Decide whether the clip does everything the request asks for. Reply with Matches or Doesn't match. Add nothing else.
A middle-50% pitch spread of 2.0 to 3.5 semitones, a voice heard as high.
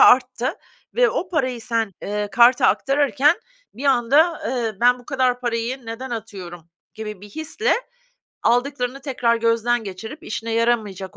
Matches